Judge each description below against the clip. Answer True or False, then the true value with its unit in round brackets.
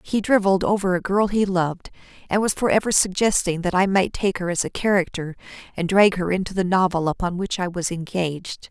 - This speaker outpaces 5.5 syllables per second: True (5.7 syllables/s)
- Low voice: False (185 Hz)